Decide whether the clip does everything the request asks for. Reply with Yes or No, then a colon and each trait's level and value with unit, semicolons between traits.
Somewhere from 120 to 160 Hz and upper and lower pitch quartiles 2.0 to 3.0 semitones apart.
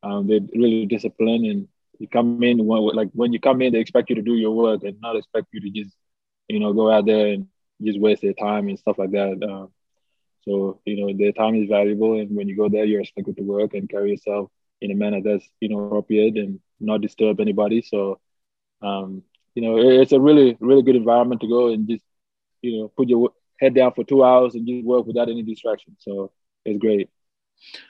No: low, 110 Hz; average, 2.7 semitones